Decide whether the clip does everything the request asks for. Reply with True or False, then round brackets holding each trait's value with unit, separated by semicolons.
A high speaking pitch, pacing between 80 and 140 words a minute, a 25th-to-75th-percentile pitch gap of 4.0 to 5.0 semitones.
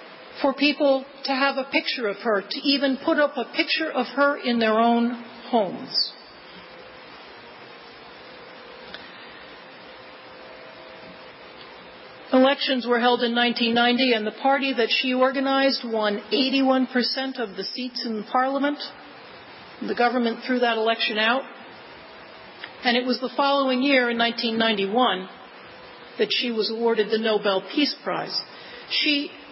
False (250 Hz; 135 wpm; 2.9 semitones)